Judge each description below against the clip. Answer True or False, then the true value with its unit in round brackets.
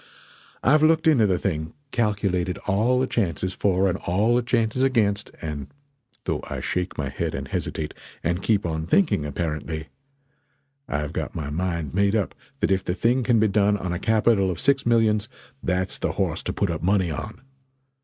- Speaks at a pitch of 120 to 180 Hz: False (100 Hz)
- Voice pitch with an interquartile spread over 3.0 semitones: True (4.6 semitones)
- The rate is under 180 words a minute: False (185 wpm)